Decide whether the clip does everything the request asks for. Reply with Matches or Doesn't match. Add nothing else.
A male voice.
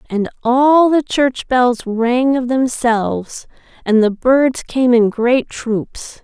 Doesn't match